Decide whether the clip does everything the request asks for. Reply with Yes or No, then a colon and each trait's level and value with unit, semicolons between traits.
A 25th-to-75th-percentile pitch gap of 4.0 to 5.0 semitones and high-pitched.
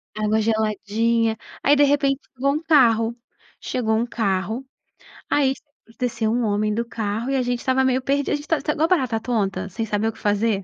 No: average, 3.5 semitones; high, 230 Hz